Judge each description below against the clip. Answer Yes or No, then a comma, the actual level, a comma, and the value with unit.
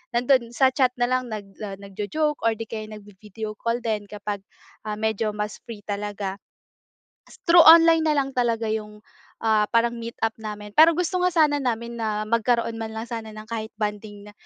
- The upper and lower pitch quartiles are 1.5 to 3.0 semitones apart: Yes, narrow, 2.6 semitones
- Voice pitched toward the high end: Yes, high, 220 Hz